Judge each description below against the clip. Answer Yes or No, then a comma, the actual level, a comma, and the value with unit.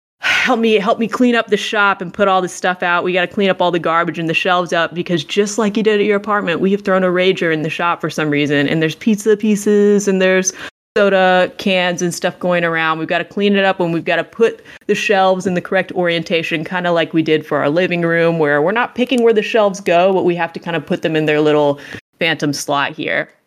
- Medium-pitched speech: Yes, medium, 180 Hz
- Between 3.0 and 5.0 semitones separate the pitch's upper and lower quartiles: Yes, average, 3.5 semitones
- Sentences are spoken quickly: Yes, fast, 270 wpm